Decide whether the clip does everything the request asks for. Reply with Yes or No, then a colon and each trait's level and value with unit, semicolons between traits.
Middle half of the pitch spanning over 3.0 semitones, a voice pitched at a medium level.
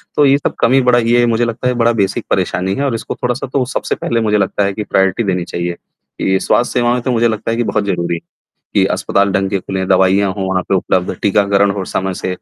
No: average, 3.9 semitones; low, 100 Hz